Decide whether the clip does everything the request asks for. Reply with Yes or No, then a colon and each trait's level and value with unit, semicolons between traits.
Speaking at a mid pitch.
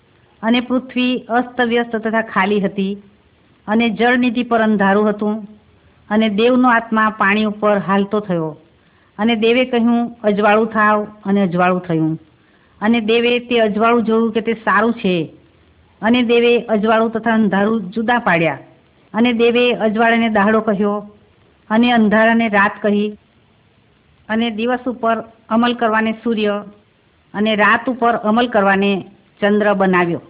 No: high, 220 Hz